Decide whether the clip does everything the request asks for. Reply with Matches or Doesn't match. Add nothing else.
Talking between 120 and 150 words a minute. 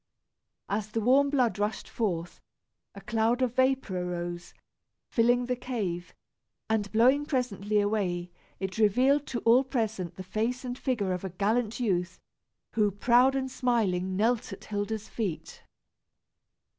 Matches